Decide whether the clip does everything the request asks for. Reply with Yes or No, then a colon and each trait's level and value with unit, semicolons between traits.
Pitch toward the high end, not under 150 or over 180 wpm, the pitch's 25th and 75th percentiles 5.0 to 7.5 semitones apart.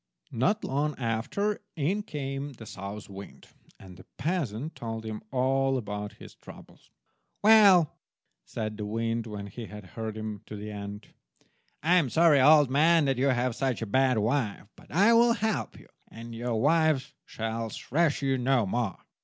No: low, 125 Hz; average, 170 wpm; wide, 5.5 semitones